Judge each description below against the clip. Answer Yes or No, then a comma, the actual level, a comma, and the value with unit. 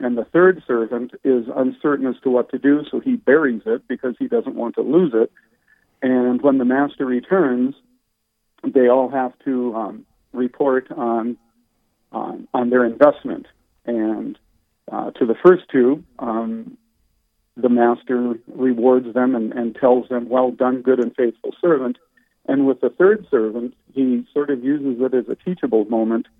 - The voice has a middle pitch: No, low, 125 Hz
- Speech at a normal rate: Yes, average, 165 wpm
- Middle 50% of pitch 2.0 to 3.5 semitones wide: Yes, narrow, 2.5 semitones